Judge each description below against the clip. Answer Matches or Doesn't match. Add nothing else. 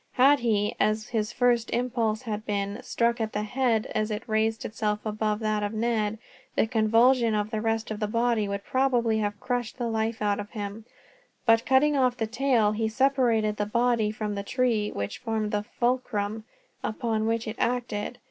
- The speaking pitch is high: Matches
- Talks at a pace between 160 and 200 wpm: Matches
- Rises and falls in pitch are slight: Matches